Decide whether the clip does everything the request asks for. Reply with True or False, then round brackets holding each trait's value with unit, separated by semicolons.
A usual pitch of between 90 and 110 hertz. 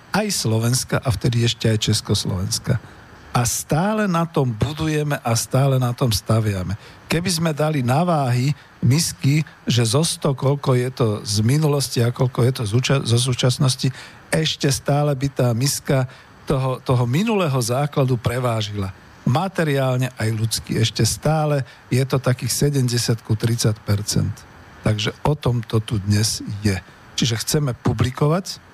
False (125 Hz)